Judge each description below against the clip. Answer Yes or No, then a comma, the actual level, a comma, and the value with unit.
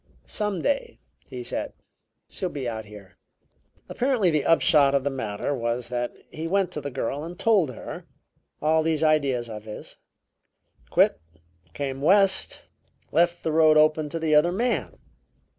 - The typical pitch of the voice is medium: Yes, medium, 155 Hz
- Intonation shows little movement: No, average, 4.6 semitones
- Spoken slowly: No, average, 155 wpm